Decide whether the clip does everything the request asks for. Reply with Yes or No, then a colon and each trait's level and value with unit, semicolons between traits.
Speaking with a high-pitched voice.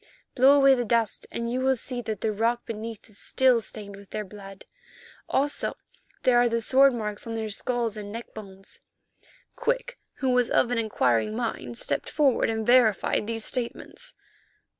Yes: high, 230 Hz